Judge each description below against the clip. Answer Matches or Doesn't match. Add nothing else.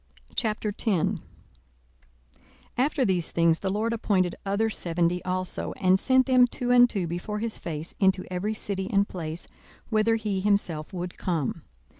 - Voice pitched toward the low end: Doesn't match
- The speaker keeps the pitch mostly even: Doesn't match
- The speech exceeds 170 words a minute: Doesn't match